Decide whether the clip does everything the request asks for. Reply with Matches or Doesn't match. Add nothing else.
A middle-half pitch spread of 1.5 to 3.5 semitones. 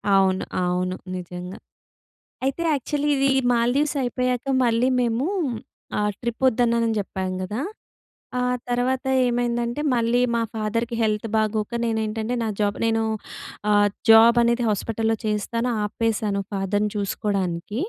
Matches